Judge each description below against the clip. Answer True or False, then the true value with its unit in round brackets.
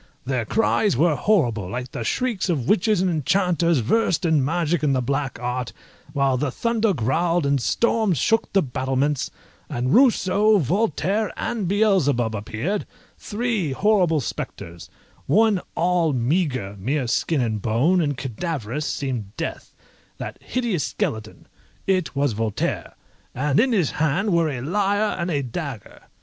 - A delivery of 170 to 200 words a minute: False (145 wpm)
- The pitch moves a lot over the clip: True (7.1 semitones)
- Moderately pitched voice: True (155 Hz)